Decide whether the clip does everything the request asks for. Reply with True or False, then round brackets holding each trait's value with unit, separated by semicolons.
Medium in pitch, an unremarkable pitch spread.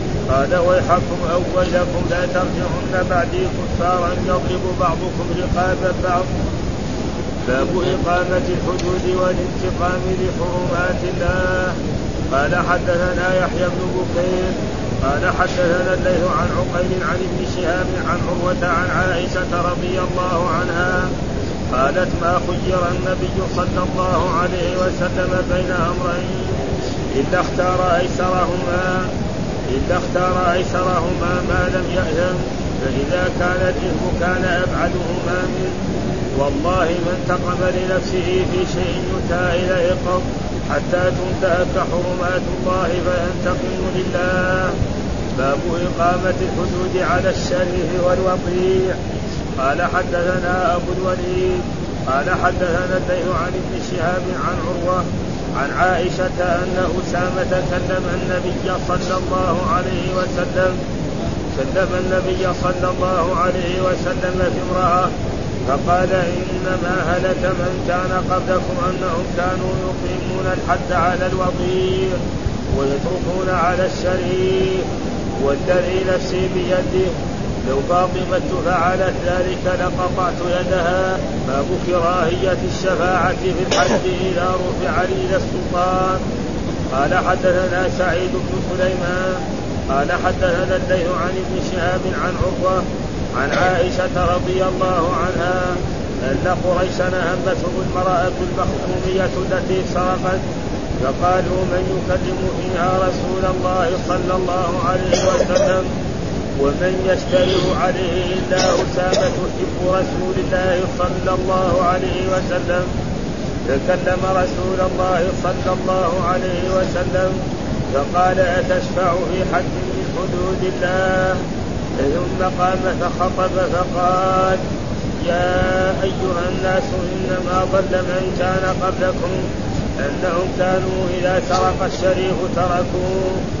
False (180 Hz; 0.8 semitones)